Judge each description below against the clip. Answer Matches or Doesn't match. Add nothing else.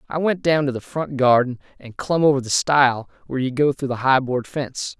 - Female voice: Doesn't match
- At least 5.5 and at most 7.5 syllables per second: Matches